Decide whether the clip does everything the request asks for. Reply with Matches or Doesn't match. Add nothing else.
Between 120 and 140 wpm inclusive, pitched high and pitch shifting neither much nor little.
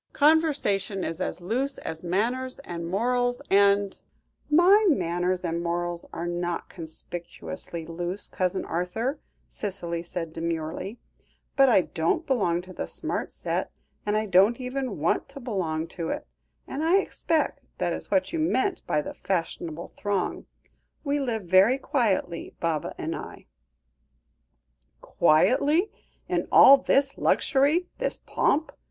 Doesn't match